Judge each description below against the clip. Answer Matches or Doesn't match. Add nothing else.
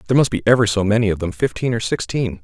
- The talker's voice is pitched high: Doesn't match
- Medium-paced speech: Doesn't match